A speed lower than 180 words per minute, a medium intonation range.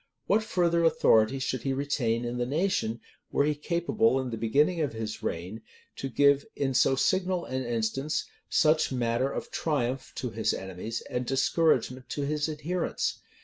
Yes: average, 165 wpm; average, 4.7 semitones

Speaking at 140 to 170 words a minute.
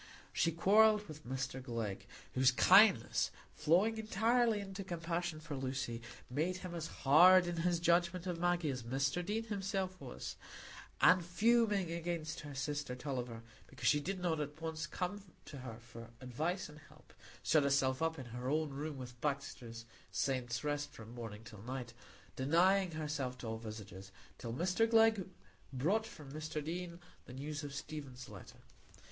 Yes: average, 160 wpm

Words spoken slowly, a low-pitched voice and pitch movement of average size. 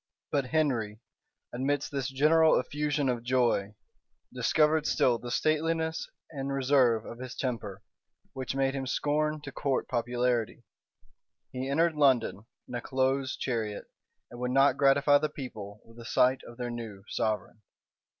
No: average, 145 wpm; low, 130 Hz; average, 3.2 semitones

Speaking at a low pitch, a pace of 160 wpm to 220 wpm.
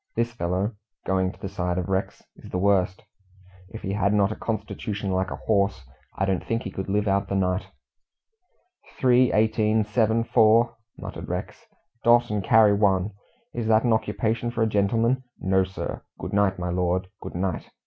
Yes: low, 100 Hz; average, 180 wpm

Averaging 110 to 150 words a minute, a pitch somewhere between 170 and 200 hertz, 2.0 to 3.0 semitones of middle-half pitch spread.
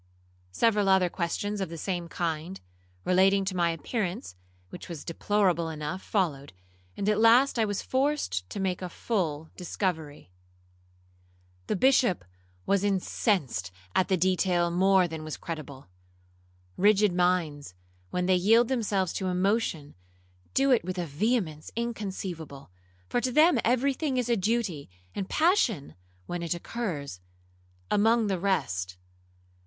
No: average, 140 wpm; medium, 185 Hz; average, 4.5 semitones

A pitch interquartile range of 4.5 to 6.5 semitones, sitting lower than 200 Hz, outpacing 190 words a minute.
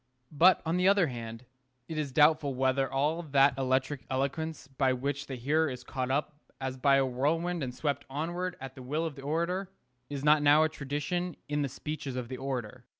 No: average, 3.1 semitones; medium, 140 Hz; fast, 205 wpm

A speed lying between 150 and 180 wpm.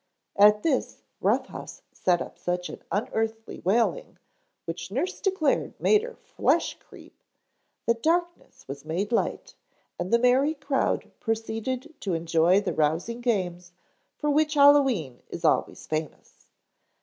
No: slow, 135 wpm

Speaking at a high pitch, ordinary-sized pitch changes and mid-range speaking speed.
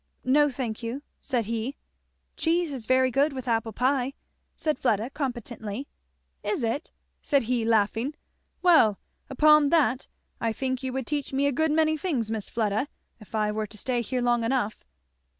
Yes: very high, 255 Hz; average, 4.0 semitones; average, 170 wpm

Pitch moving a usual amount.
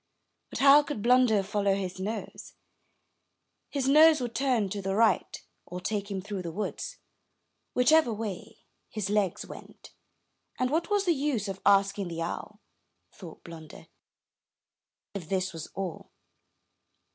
Yes: average, 5.0 semitones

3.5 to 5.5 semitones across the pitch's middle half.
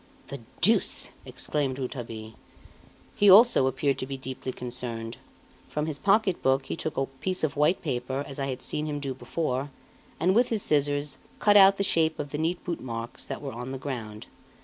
Yes: average, 3.8 semitones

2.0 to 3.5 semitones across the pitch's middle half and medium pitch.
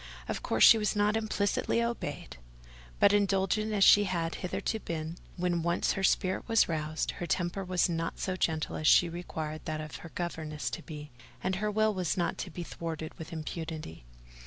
No: average, 3.9 semitones; medium, 175 Hz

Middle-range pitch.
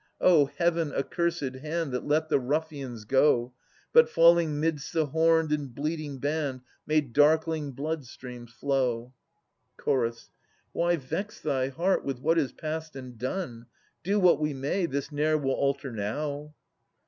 Yes: medium, 150 Hz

